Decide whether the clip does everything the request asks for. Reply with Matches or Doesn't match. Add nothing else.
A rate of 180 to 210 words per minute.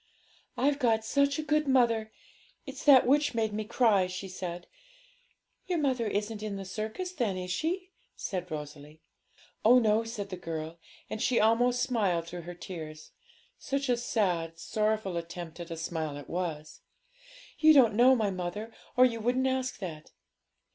Doesn't match